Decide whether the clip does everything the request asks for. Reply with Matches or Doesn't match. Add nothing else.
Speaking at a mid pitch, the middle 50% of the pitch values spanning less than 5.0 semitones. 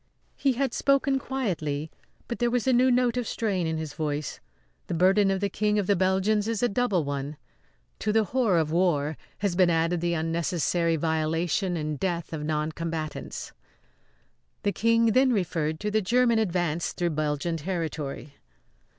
Doesn't match